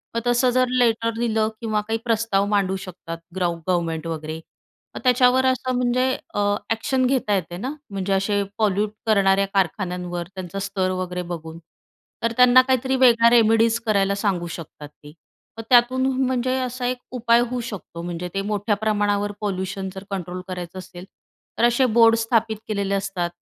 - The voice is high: Yes, high, 205 Hz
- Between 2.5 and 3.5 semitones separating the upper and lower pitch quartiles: No, average, 4.1 semitones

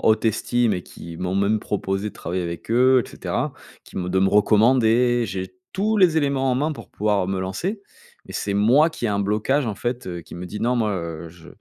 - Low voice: Yes, low, 105 Hz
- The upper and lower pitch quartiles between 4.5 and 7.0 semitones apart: Yes, average, 5.0 semitones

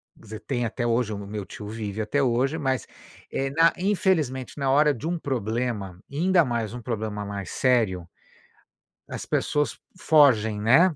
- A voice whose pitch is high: No, low, 125 Hz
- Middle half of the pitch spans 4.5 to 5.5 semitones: Yes, average, 5.2 semitones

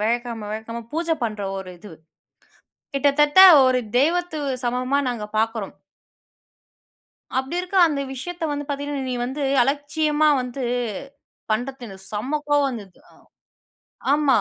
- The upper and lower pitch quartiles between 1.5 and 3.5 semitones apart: No, average, 4.3 semitones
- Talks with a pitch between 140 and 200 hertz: No, very high, 265 Hz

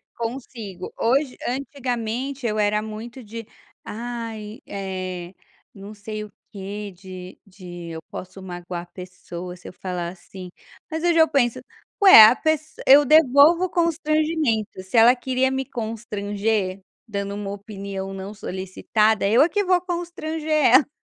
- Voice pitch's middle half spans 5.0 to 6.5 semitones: Yes, wide, 5.6 semitones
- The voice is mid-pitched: No, high, 215 Hz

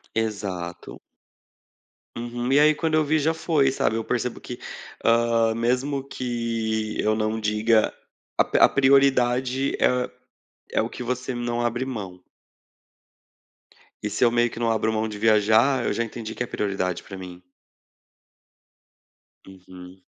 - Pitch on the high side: No, low, 115 Hz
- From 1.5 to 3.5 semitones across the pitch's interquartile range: Yes, average, 2.7 semitones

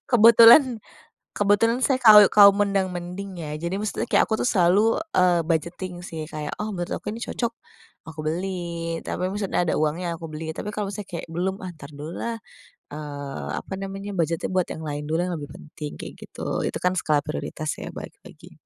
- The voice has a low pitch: No, medium, 180 Hz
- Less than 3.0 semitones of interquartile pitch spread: No, average, 4.3 semitones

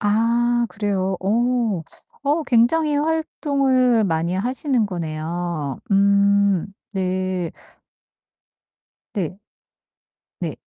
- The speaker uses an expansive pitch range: No, average, 4.8 semitones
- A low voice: No, high, 200 Hz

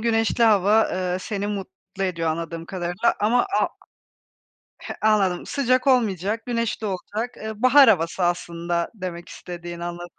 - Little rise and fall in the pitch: No, average, 4.3 semitones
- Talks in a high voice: Yes, high, 195 Hz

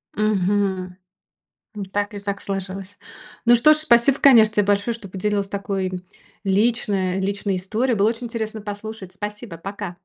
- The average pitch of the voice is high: Yes, high, 205 Hz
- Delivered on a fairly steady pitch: Yes, narrow, 2.2 semitones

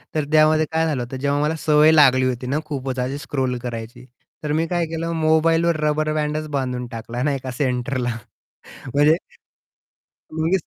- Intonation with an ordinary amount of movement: Yes, average, 3.5 semitones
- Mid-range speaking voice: Yes, medium, 145 Hz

